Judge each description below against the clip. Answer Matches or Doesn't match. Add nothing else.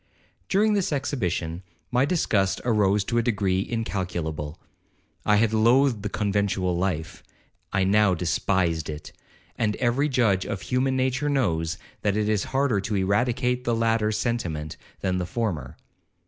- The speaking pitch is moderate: Doesn't match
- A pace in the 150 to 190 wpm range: Doesn't match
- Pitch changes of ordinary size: Matches